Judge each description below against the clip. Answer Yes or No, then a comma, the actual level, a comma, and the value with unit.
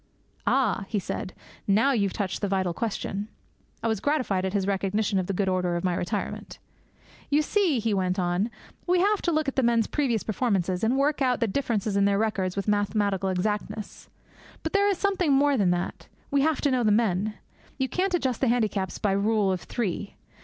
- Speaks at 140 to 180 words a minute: No, fast, 205 wpm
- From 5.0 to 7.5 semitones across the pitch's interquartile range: Yes, wide, 5.5 semitones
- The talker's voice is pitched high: Yes, high, 210 Hz